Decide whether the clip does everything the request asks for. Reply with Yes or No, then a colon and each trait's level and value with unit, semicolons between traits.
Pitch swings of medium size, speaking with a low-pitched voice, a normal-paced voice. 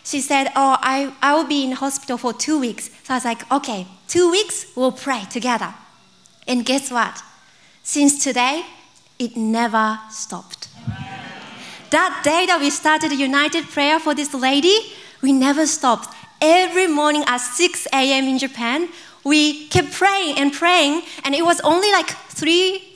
No: average, 4.3 semitones; very high, 280 Hz; average, 160 wpm